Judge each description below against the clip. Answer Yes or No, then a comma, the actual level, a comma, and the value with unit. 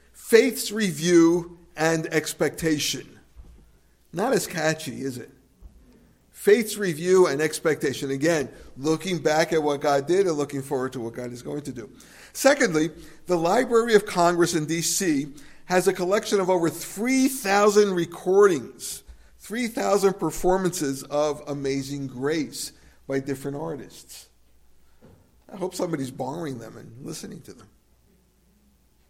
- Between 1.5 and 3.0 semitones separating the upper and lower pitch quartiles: No, wide, 5.4 semitones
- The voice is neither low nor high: Yes, medium, 160 Hz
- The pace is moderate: No, slow, 125 wpm